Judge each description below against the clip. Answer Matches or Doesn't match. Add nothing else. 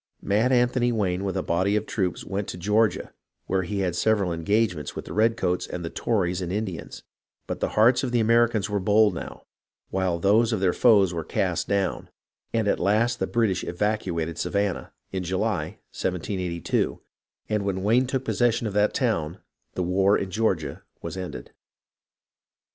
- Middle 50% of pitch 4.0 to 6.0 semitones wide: Doesn't match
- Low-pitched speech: Matches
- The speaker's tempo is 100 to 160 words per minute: Doesn't match